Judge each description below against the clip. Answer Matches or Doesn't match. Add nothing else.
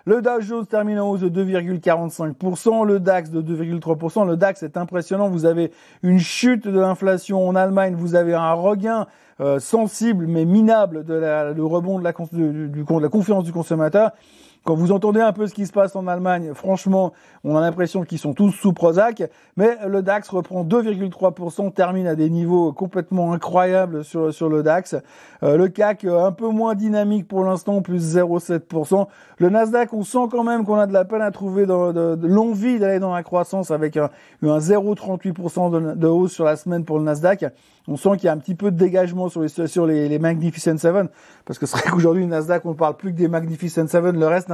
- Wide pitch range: Doesn't match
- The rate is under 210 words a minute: Doesn't match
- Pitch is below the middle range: Doesn't match